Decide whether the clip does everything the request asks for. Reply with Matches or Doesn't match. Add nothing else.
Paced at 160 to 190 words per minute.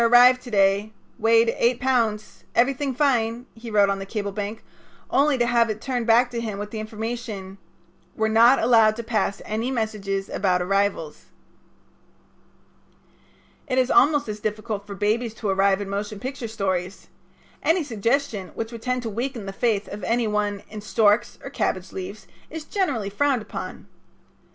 Matches